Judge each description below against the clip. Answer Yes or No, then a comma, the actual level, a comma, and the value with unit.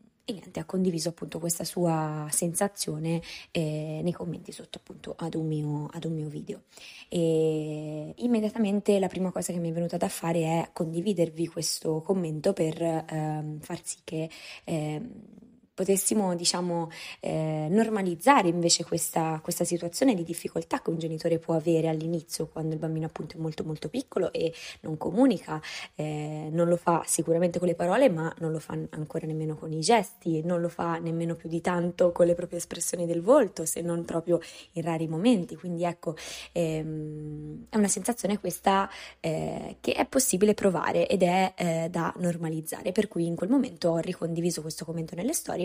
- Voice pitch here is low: No, medium, 170 Hz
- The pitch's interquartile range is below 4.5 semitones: Yes, narrow, 2.4 semitones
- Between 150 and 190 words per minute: Yes, fast, 170 wpm